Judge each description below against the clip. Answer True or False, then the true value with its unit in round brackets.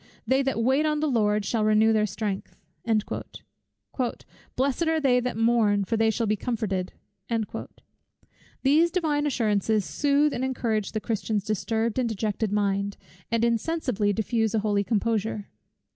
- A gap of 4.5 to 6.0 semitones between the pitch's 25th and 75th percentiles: False (3.7 semitones)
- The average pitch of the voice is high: True (225 Hz)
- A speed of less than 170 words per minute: True (145 wpm)